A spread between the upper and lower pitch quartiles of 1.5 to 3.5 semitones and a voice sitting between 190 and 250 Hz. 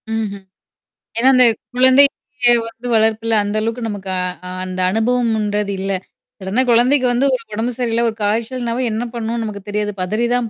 Yes: average, 2.8 semitones; high, 225 Hz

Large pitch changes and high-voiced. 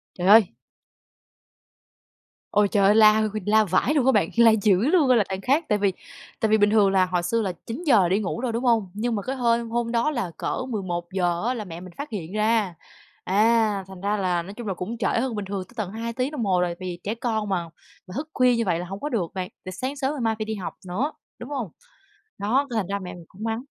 No: average, 3.8 semitones; high, 215 Hz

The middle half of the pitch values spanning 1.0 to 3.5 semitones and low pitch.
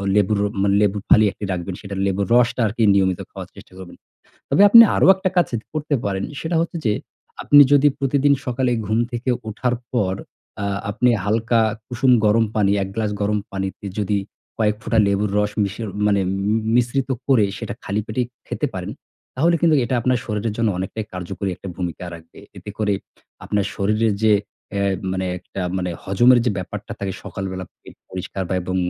No: average, 3.9 semitones; low, 105 Hz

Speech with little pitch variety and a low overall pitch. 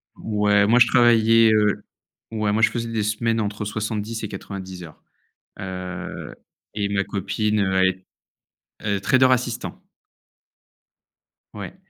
Yes: narrow, 2.2 semitones; low, 105 Hz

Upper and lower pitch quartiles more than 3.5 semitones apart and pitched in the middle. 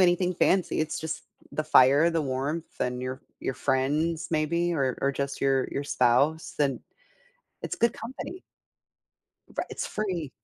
Yes: average, 4.0 semitones; medium, 155 Hz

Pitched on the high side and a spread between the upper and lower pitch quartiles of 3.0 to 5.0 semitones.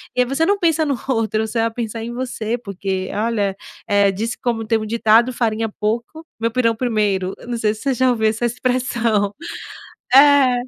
No: high, 230 Hz; narrow, 2.6 semitones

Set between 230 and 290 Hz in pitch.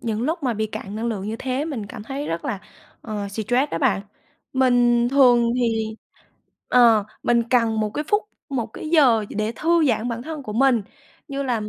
Yes: high, 240 Hz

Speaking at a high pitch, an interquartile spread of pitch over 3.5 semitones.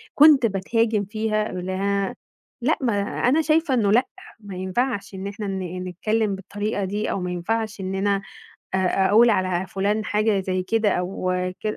No: high, 205 Hz; average, 2.9 semitones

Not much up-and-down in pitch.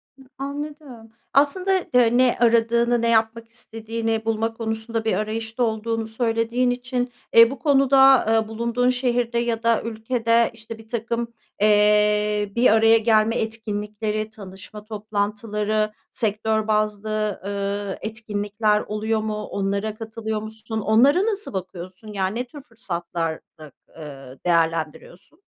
Yes: narrow, 1.9 semitones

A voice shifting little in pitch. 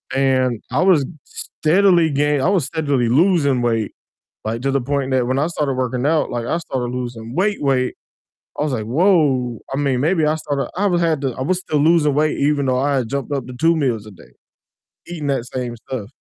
No: average, 3.8 semitones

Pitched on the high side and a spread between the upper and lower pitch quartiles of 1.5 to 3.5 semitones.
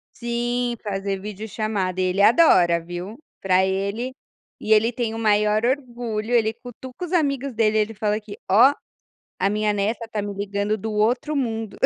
Yes: high, 215 Hz; average, 2.9 semitones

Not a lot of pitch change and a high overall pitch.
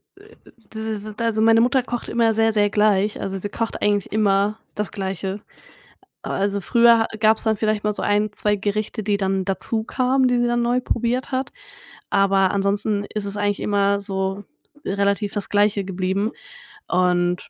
Yes: narrow, 2.0 semitones; high, 210 Hz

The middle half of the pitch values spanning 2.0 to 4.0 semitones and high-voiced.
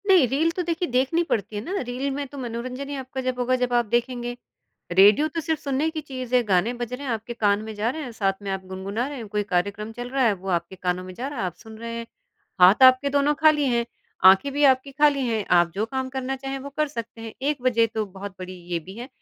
No: average, 4.8 semitones; high, 245 Hz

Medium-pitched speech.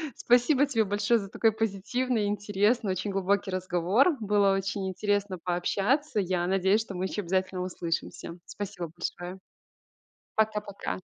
No: high, 200 Hz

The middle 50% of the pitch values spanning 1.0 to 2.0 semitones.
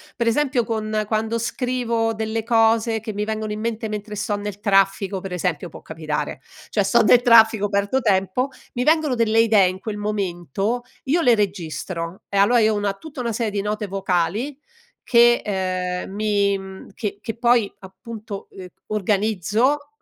No: average, 2.9 semitones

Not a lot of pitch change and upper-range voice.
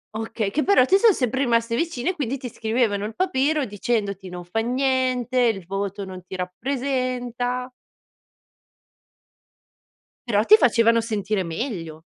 No: average, 4.3 semitones; high, 235 Hz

